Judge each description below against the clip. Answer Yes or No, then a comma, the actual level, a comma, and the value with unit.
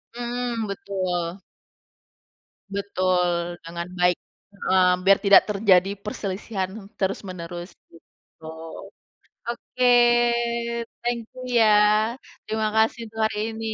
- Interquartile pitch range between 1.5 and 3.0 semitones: No, average, 3.4 semitones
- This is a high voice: Yes, high, 200 Hz